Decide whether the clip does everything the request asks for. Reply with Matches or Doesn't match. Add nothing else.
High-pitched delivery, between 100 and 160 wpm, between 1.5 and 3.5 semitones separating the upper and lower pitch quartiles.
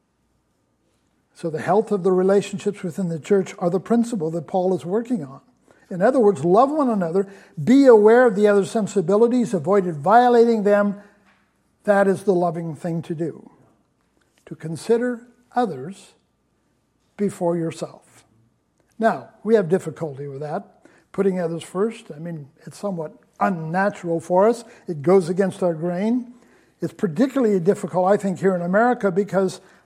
Doesn't match